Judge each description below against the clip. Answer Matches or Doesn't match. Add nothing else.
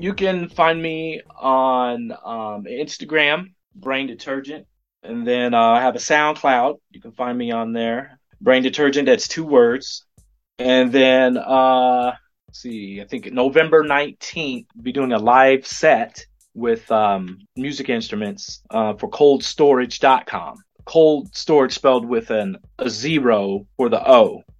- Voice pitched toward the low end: Matches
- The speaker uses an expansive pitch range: Doesn't match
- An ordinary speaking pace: Matches